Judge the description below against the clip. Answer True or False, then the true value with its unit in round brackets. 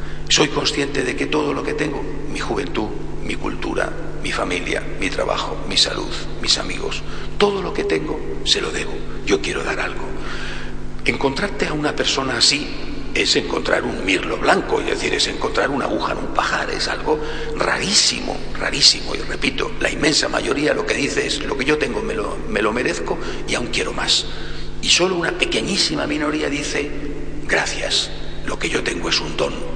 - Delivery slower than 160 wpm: False (180 wpm)